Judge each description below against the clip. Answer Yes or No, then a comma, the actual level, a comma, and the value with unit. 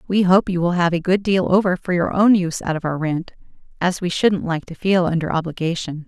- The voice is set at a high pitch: No, medium, 175 Hz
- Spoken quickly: Yes, fast, 245 wpm